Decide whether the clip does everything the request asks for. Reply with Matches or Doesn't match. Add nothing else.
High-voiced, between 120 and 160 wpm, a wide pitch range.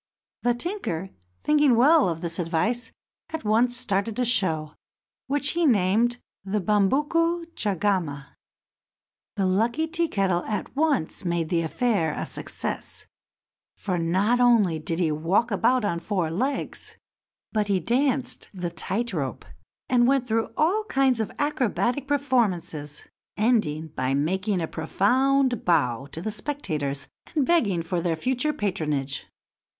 Matches